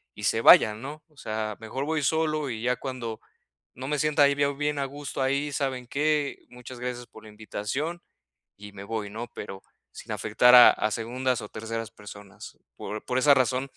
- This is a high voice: No, low, 125 Hz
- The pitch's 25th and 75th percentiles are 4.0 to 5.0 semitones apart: Yes, average, 4.4 semitones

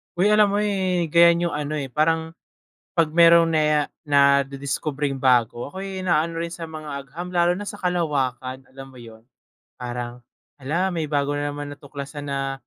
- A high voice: No, medium, 150 Hz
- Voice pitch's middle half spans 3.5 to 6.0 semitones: Yes, average, 3.8 semitones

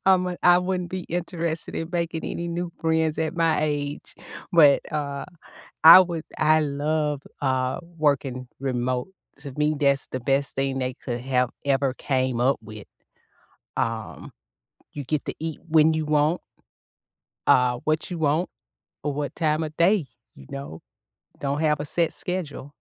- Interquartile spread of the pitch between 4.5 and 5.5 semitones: No, average, 3.1 semitones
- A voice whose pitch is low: No, medium, 150 Hz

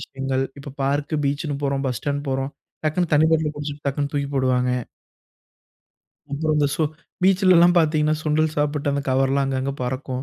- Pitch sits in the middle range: Yes, medium, 145 Hz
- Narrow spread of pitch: Yes, narrow, 2.2 semitones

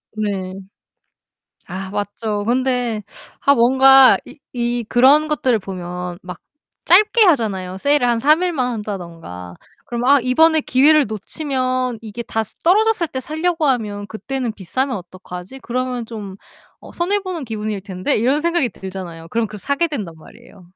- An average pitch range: No, wide, 5.9 semitones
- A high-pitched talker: Yes, high, 240 Hz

